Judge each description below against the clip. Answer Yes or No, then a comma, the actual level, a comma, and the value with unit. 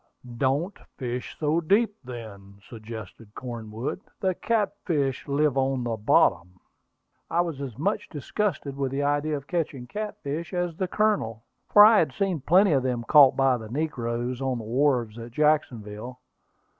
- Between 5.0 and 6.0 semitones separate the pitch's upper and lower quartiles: Yes, wide, 5.5 semitones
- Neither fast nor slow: Yes, average, 155 wpm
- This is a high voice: No, low, 135 Hz